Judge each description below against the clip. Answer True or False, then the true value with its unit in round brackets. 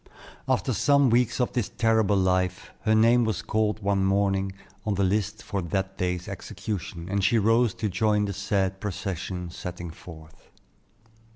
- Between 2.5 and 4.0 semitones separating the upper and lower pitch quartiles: True (2.9 semitones)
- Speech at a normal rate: True (160 wpm)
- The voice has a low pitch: True (100 Hz)